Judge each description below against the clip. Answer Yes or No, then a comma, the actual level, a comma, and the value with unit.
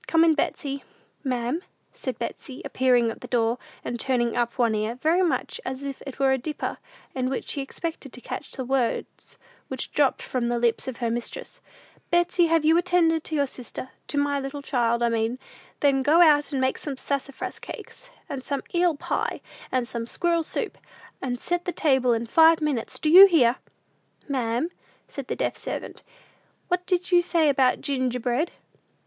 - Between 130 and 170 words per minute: No, average, 185 wpm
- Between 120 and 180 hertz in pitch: No, very high, 270 Hz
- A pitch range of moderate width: Yes, average, 4.6 semitones